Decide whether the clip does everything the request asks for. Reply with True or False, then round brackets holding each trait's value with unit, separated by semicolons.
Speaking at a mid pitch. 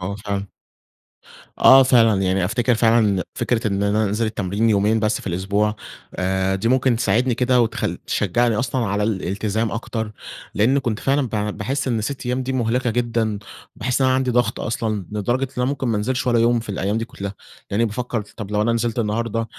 False (115 Hz)